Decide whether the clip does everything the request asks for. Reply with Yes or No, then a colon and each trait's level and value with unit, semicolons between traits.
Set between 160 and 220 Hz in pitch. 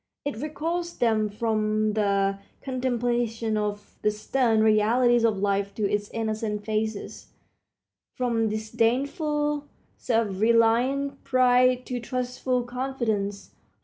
No: high, 230 Hz